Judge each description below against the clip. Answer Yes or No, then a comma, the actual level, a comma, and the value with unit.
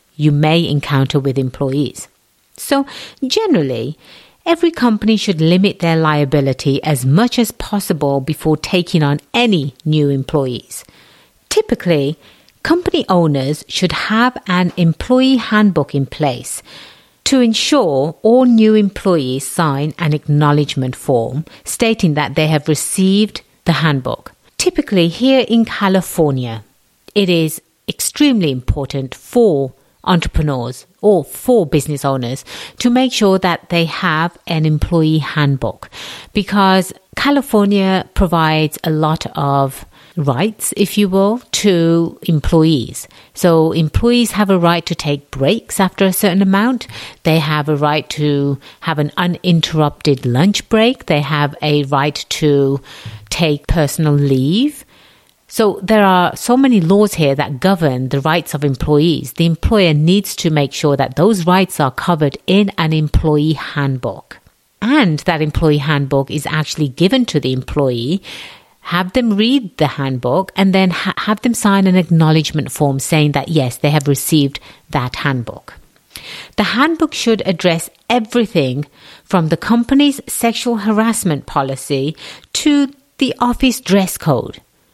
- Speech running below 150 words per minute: Yes, slow, 135 wpm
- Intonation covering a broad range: Yes, wide, 5.9 semitones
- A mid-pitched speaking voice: Yes, medium, 165 Hz